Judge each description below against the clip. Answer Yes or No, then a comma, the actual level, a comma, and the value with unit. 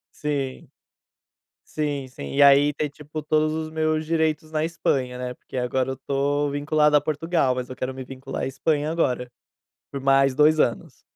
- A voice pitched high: No, medium, 145 Hz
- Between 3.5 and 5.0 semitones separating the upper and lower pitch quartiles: No, average, 2.7 semitones